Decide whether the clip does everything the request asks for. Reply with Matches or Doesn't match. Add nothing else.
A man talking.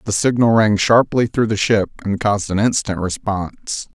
Matches